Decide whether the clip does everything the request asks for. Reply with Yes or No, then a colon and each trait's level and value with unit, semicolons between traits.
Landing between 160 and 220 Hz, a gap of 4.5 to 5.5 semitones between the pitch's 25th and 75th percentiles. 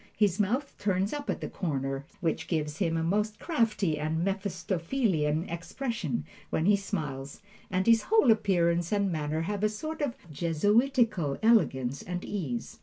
Yes: medium, 185 Hz; average, 5.2 semitones